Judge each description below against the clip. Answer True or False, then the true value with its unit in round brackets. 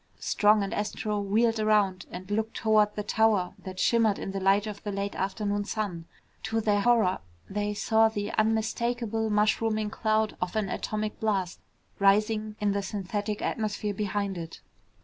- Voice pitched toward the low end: False (210 Hz)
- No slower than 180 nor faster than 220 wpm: False (160 wpm)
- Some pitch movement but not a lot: False (1.6 semitones)